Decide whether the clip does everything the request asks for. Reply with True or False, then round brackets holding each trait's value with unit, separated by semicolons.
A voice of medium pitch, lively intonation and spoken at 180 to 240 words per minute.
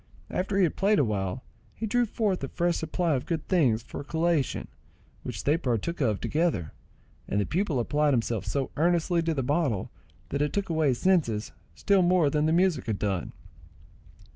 True (155 Hz; 6.2 semitones; 190 wpm)